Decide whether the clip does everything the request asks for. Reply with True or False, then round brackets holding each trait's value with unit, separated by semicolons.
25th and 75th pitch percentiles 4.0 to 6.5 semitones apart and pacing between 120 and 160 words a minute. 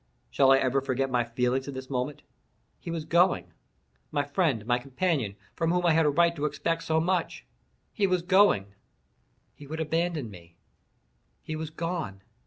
True (5.4 semitones; 155 wpm)